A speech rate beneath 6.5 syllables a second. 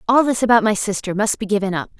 No: 6.7 syllables/s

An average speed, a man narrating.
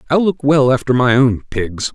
No: fast, 215 wpm; male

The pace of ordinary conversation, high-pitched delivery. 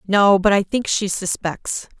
Yes: average, 180 wpm; high, 195 Hz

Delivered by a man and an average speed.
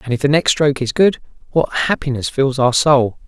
No: male; fast, 220 wpm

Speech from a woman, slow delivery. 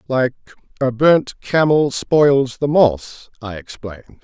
No: male; slow, 130 wpm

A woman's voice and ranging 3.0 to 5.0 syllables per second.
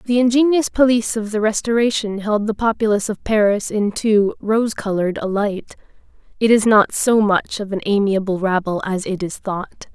No: female; 5.2 syllables/s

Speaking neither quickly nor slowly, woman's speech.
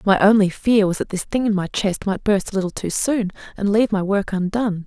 No: fast, 260 wpm; female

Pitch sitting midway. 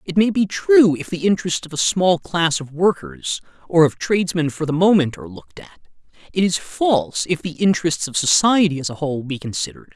Yes: medium, 165 Hz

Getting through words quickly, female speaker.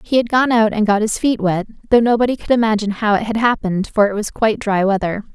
Yes: fast, 260 wpm; female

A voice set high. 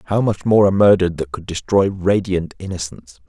No: very low, 95 Hz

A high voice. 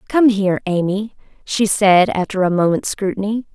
Yes: high, 200 Hz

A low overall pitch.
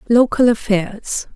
No: high, 220 Hz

